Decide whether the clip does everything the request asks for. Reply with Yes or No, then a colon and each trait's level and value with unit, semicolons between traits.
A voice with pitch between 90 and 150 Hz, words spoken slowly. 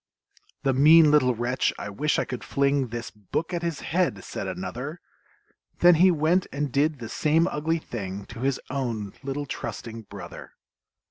No: medium, 140 Hz; average, 170 wpm